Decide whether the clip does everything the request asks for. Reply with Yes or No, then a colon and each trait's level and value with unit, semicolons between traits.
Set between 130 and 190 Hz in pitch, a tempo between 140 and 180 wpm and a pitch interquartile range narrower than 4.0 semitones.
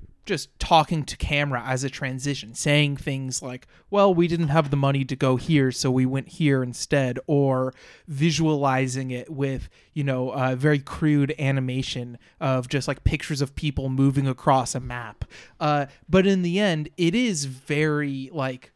Yes: medium, 140 Hz; average, 170 wpm; narrow, 2.6 semitones